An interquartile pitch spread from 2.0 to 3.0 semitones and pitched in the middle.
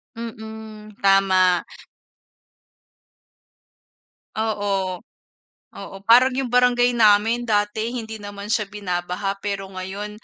No: narrow, 2.6 semitones; high, 210 Hz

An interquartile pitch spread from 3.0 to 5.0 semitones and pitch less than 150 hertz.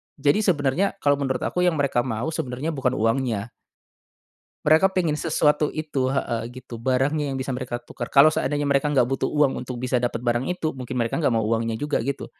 Yes: average, 3.4 semitones; low, 135 Hz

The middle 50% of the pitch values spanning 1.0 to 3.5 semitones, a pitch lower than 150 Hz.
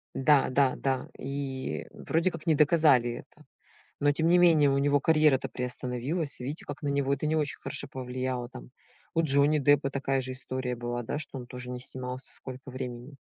Yes: narrow, 2.5 semitones; low, 135 Hz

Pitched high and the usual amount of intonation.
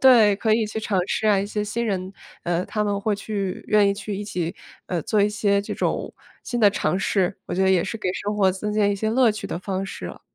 No: high, 205 Hz; narrow, 1.9 semitones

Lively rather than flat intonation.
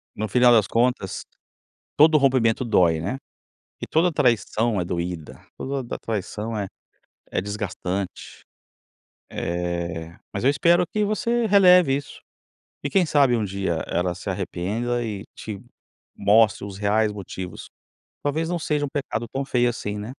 Yes: wide, 6.1 semitones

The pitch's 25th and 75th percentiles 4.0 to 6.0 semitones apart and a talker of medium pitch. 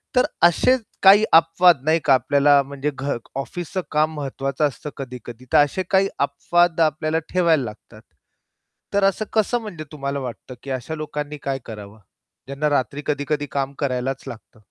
No: average, 3.5 semitones; medium, 145 Hz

